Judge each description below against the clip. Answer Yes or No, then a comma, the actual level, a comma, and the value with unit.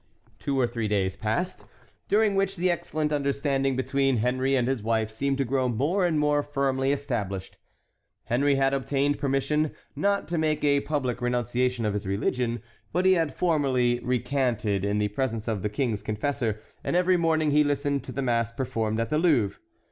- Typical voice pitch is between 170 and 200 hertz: No, low, 135 Hz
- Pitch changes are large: No, average, 4.0 semitones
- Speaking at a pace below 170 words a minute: No, average, 180 wpm